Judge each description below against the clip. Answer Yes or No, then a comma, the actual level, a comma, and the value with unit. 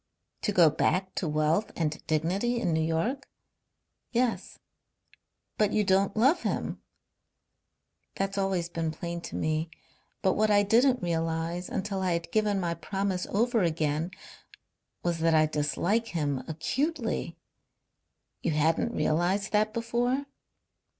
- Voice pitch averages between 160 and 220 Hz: Yes, medium, 185 Hz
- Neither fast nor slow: No, slow, 130 wpm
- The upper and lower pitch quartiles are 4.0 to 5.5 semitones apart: Yes, average, 4.8 semitones